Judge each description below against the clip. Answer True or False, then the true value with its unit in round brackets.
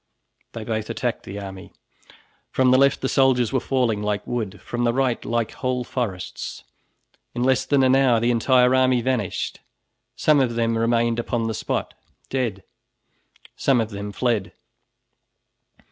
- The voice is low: True (120 Hz)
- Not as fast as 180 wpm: True (155 wpm)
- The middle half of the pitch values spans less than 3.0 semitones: True (2.6 semitones)